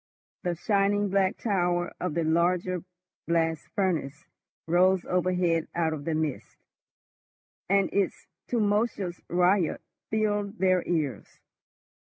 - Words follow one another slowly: Yes, slow, 110 wpm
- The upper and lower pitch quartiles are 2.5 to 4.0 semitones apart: Yes, average, 2.9 semitones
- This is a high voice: No, medium, 180 Hz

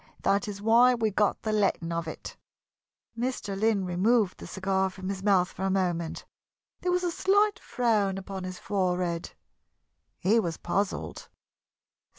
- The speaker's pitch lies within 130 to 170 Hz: No, high, 195 Hz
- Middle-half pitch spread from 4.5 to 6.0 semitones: No, average, 3.3 semitones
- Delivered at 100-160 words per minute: Yes, average, 155 wpm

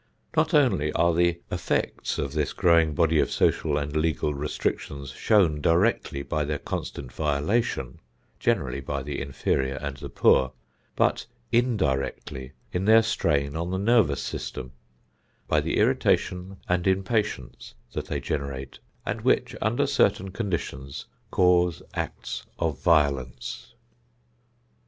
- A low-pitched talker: Yes, very low, 75 Hz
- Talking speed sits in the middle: No, slow, 130 wpm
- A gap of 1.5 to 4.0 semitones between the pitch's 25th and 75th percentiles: No, average, 4.5 semitones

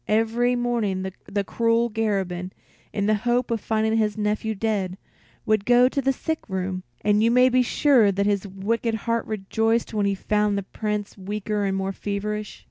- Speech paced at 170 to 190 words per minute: Yes, average, 180 wpm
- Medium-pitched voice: No, high, 210 Hz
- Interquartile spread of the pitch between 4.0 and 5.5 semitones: No, narrow, 2.5 semitones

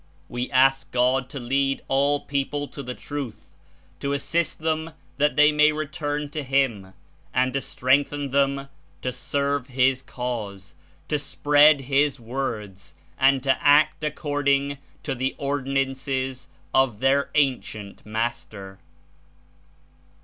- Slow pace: Yes, slow, 125 wpm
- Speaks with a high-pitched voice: No, low, 135 Hz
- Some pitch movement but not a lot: No, narrow, 2.2 semitones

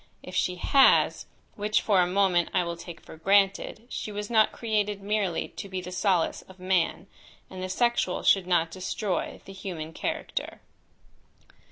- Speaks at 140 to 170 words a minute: Yes, average, 165 wpm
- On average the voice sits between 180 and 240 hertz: Yes, high, 190 Hz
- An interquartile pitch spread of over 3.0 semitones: No, narrow, 2.5 semitones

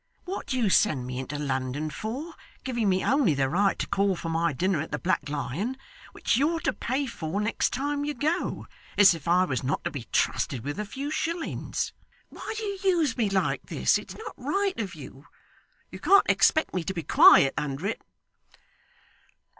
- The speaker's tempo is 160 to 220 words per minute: Yes, average, 195 wpm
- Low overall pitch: No, high, 195 Hz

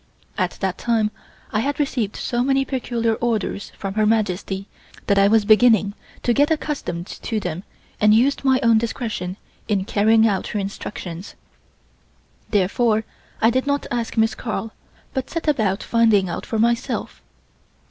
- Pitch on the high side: Yes, high, 220 Hz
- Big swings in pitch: No, average, 3.2 semitones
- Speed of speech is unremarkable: Yes, average, 155 wpm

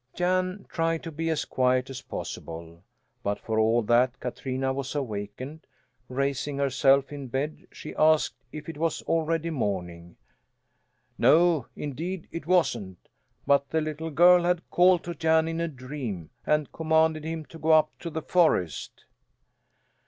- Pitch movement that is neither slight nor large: Yes, average, 4.4 semitones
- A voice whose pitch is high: No, medium, 150 Hz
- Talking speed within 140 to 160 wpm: Yes, average, 150 wpm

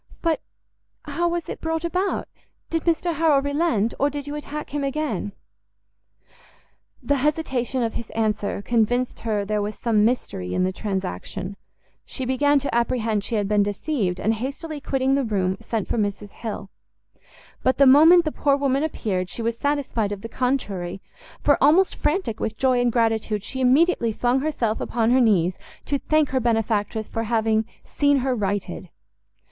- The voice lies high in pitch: Yes, high, 245 Hz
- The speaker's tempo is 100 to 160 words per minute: No, average, 170 wpm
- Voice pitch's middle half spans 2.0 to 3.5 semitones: No, average, 5.2 semitones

